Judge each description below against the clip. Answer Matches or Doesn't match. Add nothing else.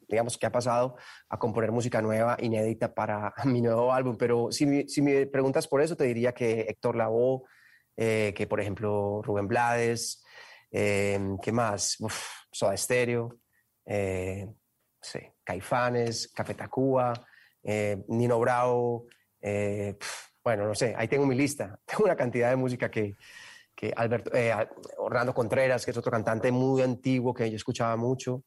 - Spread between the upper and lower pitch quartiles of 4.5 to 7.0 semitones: Doesn't match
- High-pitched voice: Doesn't match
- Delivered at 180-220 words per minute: Doesn't match